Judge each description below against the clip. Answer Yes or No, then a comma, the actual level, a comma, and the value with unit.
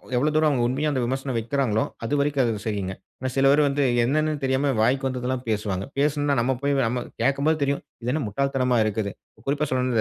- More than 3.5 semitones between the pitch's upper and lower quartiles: No, average, 3.2 semitones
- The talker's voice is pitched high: No, low, 130 Hz